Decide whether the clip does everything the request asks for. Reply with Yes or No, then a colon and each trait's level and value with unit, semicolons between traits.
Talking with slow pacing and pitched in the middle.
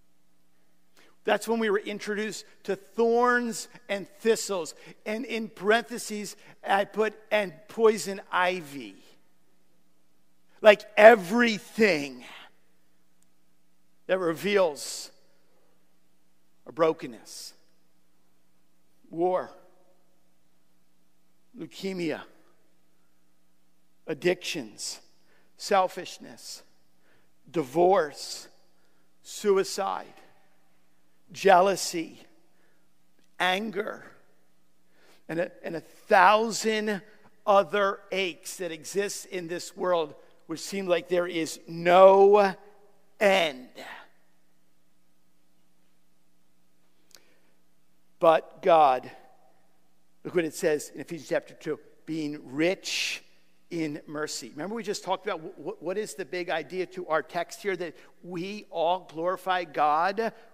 Yes: slow, 80 wpm; medium, 165 Hz